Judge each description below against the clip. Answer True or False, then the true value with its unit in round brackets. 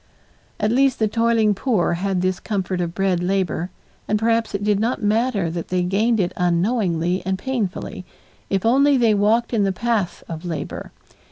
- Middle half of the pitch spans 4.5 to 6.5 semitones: False (4.1 semitones)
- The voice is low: False (200 Hz)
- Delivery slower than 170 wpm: False (175 wpm)